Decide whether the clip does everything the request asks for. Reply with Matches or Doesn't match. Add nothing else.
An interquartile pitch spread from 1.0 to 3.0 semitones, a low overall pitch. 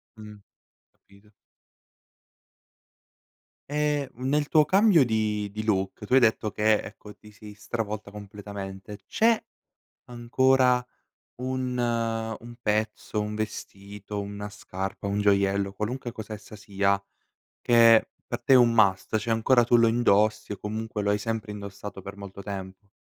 Matches